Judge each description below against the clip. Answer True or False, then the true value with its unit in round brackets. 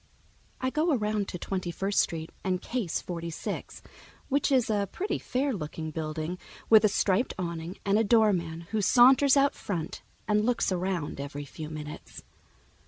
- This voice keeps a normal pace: True (165 wpm)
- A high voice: True (195 Hz)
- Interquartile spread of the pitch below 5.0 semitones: False (5.6 semitones)